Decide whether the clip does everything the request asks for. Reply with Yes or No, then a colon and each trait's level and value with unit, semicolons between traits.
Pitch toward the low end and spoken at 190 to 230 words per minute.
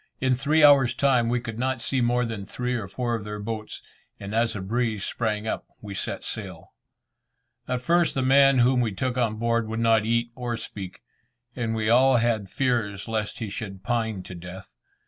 Yes: low, 115 Hz; average, 200 wpm